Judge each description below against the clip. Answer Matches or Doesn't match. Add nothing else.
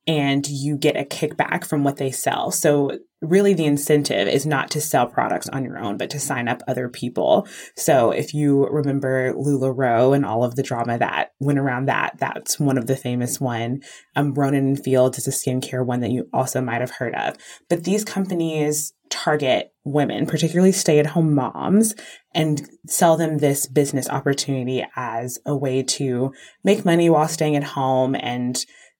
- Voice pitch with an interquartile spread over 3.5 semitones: Doesn't match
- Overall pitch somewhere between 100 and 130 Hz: Doesn't match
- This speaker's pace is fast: Doesn't match